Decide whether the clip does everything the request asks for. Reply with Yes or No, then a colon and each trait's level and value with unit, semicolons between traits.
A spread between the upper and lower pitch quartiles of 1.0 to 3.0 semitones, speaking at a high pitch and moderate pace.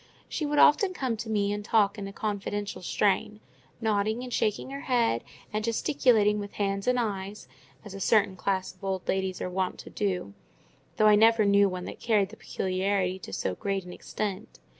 Yes: narrow, 2.4 semitones; high, 205 Hz; average, 195 wpm